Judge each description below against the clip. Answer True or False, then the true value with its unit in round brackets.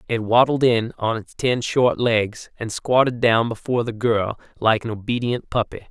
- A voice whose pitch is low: True (115 Hz)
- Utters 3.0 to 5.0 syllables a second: True (4.6 syllables/s)